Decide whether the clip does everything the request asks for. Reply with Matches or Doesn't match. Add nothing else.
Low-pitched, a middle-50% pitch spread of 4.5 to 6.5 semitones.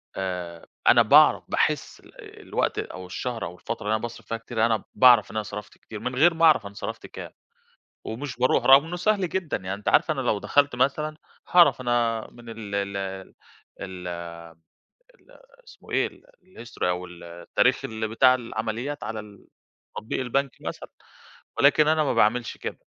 Matches